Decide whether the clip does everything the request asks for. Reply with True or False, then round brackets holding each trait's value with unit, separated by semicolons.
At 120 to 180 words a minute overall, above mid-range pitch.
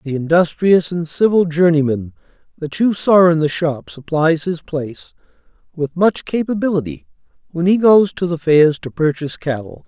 False (160 wpm; 165 Hz)